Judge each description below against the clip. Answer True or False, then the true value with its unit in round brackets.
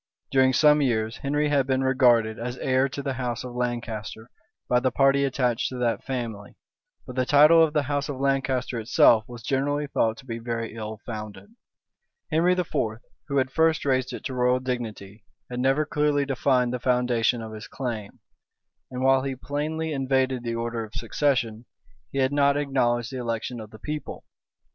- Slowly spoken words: False (180 wpm)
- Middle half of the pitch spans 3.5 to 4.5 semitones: False (2.9 semitones)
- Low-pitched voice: True (130 Hz)